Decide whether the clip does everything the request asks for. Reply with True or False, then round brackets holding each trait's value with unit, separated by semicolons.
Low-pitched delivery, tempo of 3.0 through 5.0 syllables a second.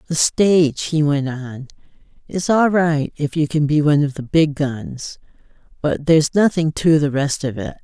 False (150 Hz; 4.6 syllables/s)